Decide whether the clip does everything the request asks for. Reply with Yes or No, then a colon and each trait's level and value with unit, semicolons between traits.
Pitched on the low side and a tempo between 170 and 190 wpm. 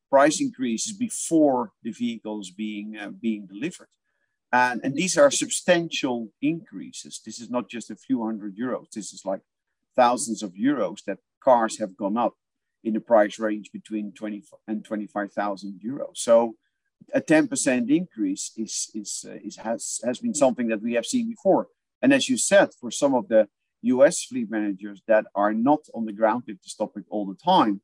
Yes: low, 120 Hz; average, 180 wpm